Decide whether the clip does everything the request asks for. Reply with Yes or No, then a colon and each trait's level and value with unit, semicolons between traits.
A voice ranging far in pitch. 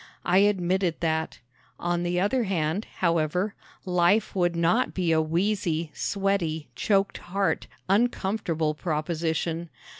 No: average, 3.2 semitones